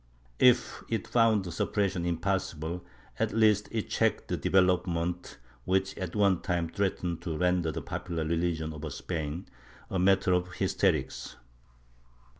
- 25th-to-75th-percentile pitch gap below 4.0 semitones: Yes, narrow, 2.6 semitones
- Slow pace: Yes, slow, 130 wpm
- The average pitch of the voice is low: Yes, very low, 90 Hz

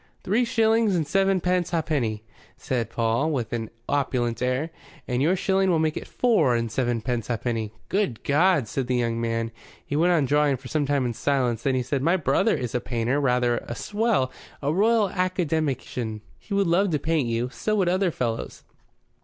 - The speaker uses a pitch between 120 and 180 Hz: Yes, medium, 140 Hz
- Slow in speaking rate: No, average, 185 wpm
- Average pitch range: No, wide, 6.9 semitones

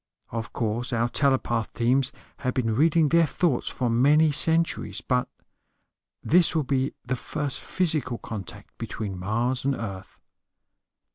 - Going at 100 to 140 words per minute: Yes, slow, 135 wpm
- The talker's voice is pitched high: No, low, 130 Hz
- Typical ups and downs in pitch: Yes, average, 4.4 semitones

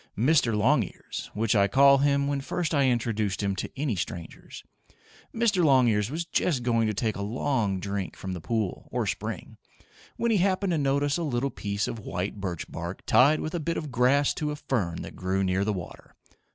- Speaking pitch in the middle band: No, low, 120 Hz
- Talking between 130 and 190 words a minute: No, average, 200 wpm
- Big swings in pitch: Yes, wide, 6.3 semitones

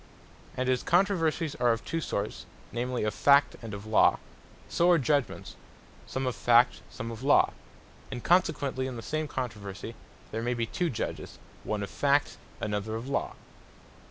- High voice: No, low, 125 Hz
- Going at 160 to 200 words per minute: Yes, average, 165 wpm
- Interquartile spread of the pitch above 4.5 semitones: No, average, 4.2 semitones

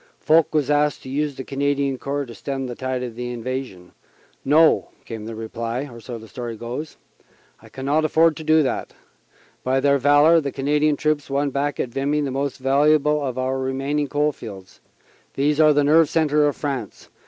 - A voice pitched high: No, medium, 140 Hz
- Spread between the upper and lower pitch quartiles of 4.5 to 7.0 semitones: No, narrow, 2.6 semitones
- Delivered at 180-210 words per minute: Yes, average, 185 wpm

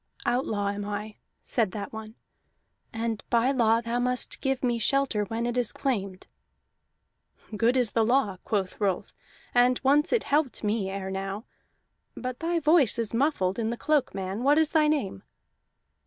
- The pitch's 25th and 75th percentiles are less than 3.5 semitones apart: No, average, 4.4 semitones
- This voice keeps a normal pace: Yes, average, 165 wpm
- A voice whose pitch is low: No, high, 230 Hz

